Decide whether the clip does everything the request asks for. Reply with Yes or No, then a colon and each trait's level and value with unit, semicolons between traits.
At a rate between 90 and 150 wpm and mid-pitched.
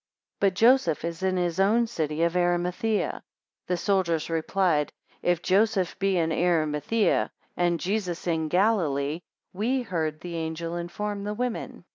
Yes: average, 145 wpm; medium, 175 Hz